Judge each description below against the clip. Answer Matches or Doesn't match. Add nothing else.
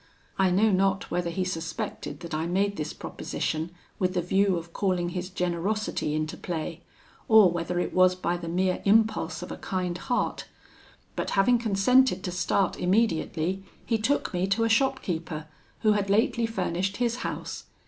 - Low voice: Doesn't match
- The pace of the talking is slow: Doesn't match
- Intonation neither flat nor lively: Matches